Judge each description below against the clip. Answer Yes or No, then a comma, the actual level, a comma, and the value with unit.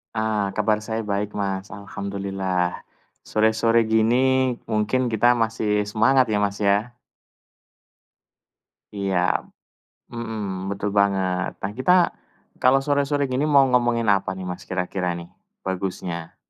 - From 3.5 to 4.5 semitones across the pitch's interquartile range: No, average, 3.1 semitones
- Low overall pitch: Yes, low, 105 Hz